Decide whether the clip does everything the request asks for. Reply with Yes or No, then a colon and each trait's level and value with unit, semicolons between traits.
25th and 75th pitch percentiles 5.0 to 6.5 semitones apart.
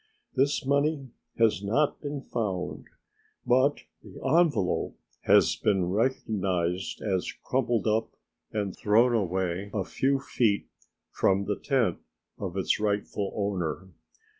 Yes: wide, 5.5 semitones